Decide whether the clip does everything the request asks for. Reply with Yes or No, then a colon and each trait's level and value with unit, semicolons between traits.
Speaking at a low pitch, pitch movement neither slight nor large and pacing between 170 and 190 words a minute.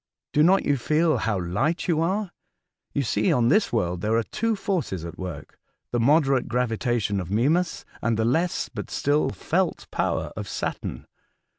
No: low, 125 Hz; wide, 7.5 semitones; average, 175 wpm